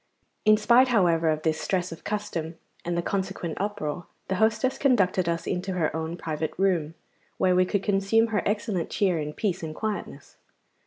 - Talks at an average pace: Yes, average, 175 wpm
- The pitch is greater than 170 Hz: Yes, medium, 185 Hz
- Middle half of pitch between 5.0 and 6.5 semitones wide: No, average, 4.0 semitones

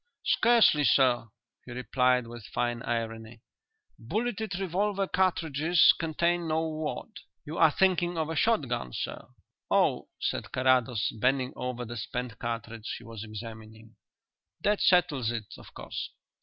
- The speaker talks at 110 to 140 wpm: Yes, slow, 135 wpm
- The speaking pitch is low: Yes, low, 130 Hz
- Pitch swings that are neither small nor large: No, wide, 6.9 semitones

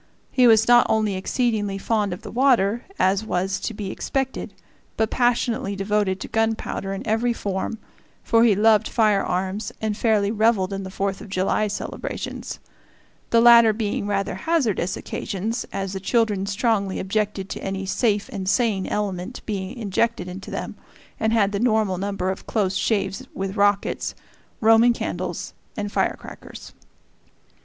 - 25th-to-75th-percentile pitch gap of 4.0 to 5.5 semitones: No, narrow, 2.6 semitones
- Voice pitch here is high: Yes, high, 205 Hz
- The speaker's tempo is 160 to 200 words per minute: No, average, 150 wpm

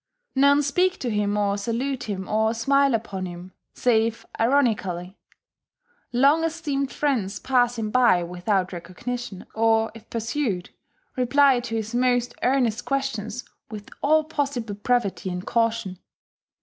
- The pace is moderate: No, slow, 130 wpm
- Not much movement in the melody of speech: No, average, 4.7 semitones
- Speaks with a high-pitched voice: Yes, high, 230 Hz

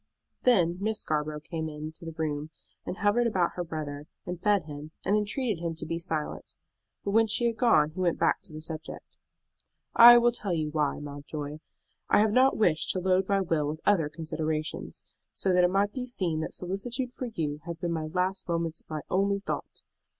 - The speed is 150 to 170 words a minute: No, average, 200 wpm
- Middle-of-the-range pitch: Yes, medium, 170 Hz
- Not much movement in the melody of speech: No, average, 4.7 semitones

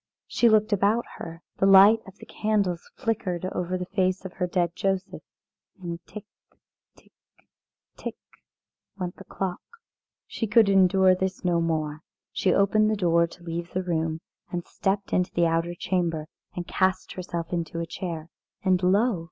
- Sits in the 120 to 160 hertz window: No, medium, 185 Hz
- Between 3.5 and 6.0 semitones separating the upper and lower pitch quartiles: No, narrow, 2.4 semitones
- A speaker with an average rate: Yes, average, 160 wpm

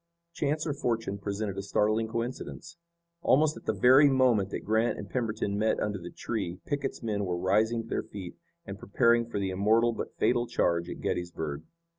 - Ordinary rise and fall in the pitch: Yes, average, 3.4 semitones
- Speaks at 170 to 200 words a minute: Yes, average, 185 wpm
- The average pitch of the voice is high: No, low, 110 Hz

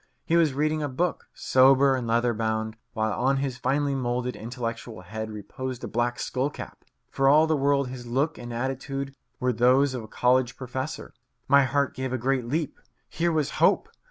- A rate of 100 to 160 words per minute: No, average, 185 wpm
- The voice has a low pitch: Yes, low, 130 Hz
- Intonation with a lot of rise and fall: No, narrow, 2.5 semitones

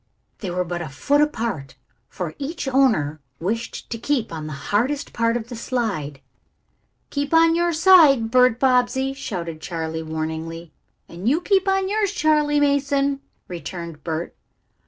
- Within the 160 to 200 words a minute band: No, average, 150 wpm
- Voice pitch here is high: Yes, high, 235 Hz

